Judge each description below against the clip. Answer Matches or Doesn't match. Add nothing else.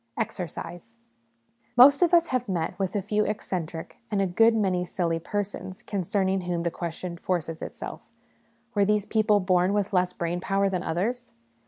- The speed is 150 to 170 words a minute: Matches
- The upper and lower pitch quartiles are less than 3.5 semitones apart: Matches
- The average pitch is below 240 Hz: Matches